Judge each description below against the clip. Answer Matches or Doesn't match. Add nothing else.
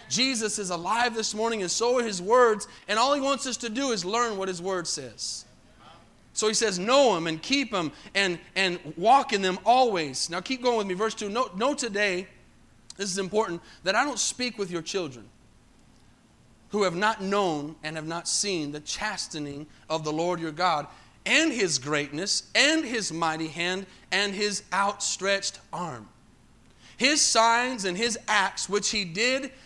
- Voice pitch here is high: Matches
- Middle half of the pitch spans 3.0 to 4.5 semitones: Doesn't match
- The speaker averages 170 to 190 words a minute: Matches